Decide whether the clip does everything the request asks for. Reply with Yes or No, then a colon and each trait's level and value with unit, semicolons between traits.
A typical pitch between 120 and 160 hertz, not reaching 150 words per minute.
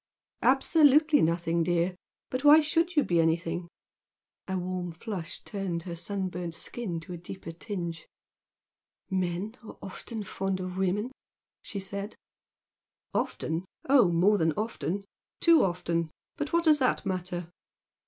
No: medium, 185 Hz; slow, 135 wpm